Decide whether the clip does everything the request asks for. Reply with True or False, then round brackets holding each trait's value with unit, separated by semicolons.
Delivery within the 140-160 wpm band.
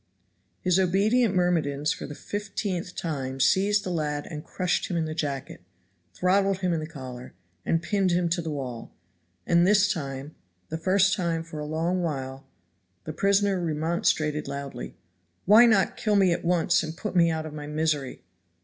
False (175 wpm)